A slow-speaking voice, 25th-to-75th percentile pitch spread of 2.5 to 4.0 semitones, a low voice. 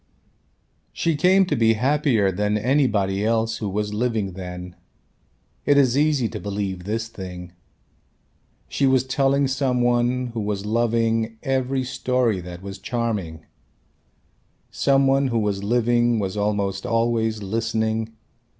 Yes: slow, 130 wpm; average, 3.7 semitones; low, 115 Hz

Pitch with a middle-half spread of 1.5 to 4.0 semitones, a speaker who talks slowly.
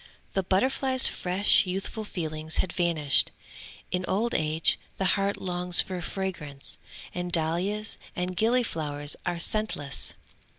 Yes: average, 3.7 semitones; slow, 120 wpm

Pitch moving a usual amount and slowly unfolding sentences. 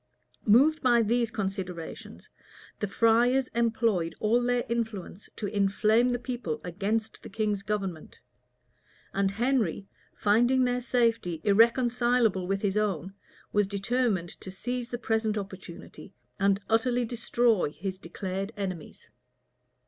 Yes: average, 3.7 semitones; slow, 120 wpm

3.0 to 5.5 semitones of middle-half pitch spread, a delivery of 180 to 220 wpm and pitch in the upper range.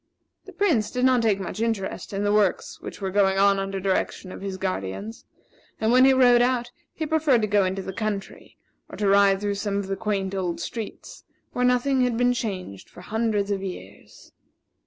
Yes: average, 3.8 semitones; average, 200 wpm; high, 205 Hz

